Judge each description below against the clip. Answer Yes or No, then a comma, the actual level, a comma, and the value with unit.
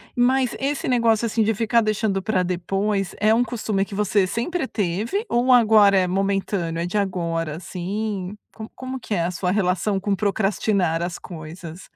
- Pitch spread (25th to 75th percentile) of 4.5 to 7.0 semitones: No, average, 3.6 semitones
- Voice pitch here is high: Yes, high, 200 Hz